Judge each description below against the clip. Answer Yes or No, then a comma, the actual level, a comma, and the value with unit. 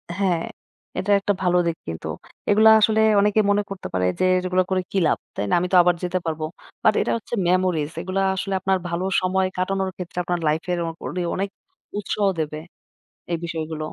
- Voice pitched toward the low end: No, medium, 185 Hz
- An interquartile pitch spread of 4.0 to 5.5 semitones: No, narrow, 2.5 semitones